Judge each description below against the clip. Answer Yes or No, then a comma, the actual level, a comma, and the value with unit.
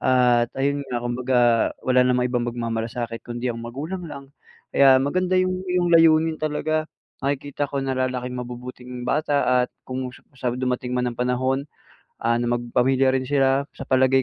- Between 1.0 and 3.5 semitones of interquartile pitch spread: Yes, narrow, 2.4 semitones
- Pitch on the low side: Yes, low, 130 Hz